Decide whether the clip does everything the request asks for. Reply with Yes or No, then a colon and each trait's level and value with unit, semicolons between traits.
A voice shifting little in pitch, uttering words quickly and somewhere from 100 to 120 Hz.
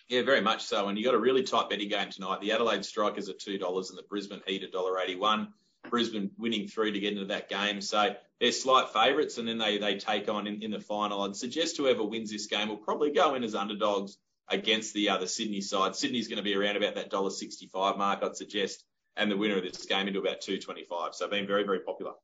Yes: narrow, 1.6 semitones; fast, 260 wpm; low, 105 Hz